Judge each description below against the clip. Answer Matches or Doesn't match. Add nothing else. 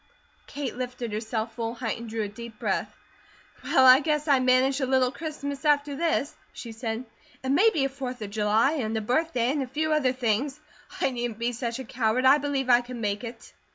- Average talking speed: Doesn't match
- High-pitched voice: Matches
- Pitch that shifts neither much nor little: Matches